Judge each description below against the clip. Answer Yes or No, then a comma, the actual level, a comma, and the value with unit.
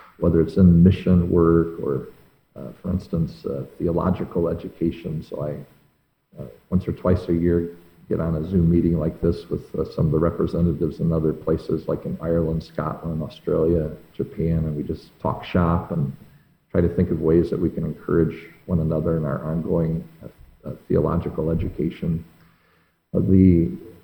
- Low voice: Yes, very low, 85 Hz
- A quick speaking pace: No, average, 170 wpm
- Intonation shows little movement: Yes, narrow, 1.1 semitones